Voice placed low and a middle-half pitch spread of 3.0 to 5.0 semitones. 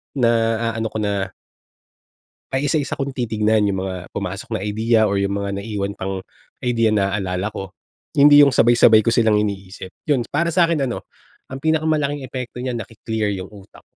Yes: low, 110 Hz; average, 4.3 semitones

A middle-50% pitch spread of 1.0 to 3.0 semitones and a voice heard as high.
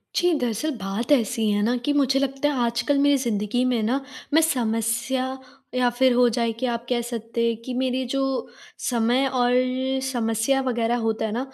Yes: narrow, 2.5 semitones; high, 245 Hz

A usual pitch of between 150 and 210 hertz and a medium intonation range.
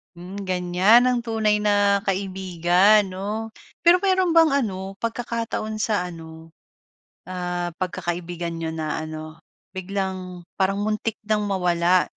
Yes: high, 190 Hz; average, 3.4 semitones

